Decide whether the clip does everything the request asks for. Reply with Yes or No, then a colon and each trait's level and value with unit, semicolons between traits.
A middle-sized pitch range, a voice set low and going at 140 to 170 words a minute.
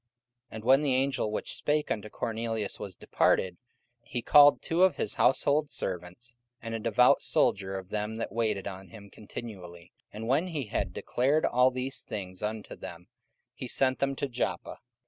No: average, 4.7 semitones; low, 115 Hz; average, 180 wpm